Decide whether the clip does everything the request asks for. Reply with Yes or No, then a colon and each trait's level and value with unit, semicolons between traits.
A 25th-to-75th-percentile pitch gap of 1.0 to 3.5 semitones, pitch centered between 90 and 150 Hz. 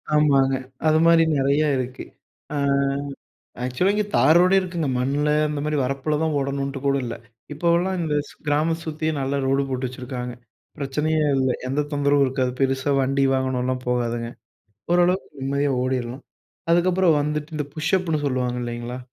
Yes: average, 3.2 semitones; medium, 140 Hz